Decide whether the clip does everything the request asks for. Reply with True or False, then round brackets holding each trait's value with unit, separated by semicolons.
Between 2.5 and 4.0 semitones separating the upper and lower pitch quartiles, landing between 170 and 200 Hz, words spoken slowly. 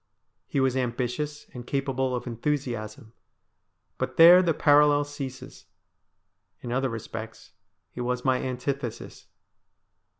False (2.9 semitones; 130 Hz; 110 wpm)